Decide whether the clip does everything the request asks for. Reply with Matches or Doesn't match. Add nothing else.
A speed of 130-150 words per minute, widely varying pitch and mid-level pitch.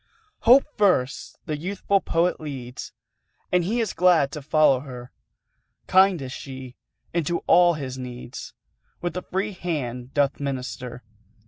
Matches